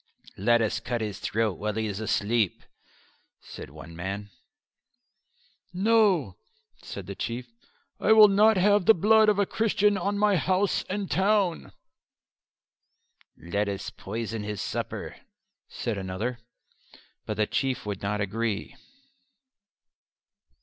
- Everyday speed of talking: No, slow, 125 wpm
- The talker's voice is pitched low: Yes, low, 115 Hz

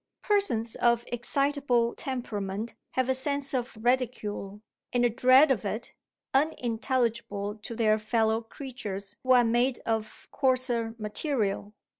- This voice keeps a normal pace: No, slow, 125 wpm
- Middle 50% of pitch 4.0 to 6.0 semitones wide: No, average, 3.0 semitones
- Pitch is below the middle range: No, high, 235 Hz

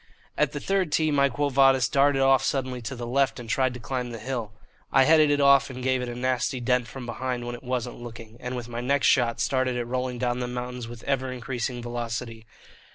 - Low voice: Yes, low, 125 Hz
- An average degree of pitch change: No, narrow, 1.8 semitones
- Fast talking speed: Yes, fast, 230 wpm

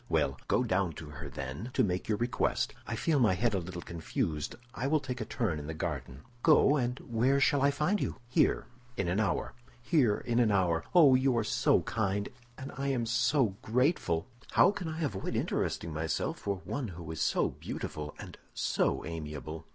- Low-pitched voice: Yes, low, 110 Hz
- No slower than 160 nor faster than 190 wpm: No, average, 200 wpm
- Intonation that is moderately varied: No, wide, 7.9 semitones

